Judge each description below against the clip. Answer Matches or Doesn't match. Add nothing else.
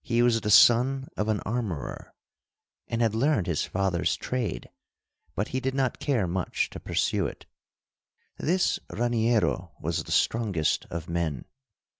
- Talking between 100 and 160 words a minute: Matches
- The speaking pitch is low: Matches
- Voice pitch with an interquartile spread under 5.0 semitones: Doesn't match